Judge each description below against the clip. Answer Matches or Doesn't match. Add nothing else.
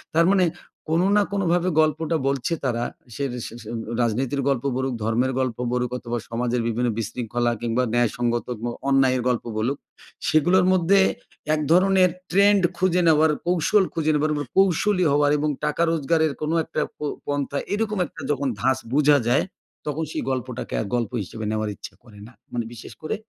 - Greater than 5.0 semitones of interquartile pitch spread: Matches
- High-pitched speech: Doesn't match